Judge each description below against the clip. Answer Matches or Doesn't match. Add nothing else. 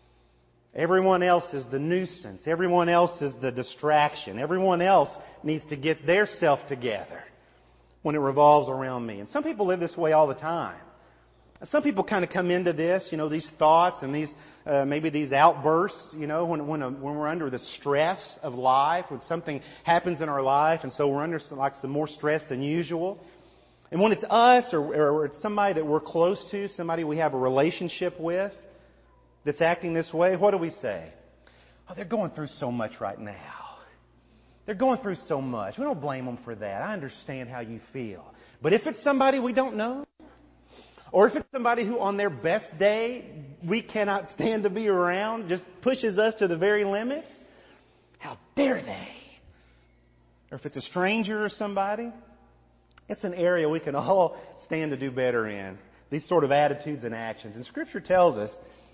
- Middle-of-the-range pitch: Matches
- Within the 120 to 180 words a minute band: Doesn't match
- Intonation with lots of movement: Matches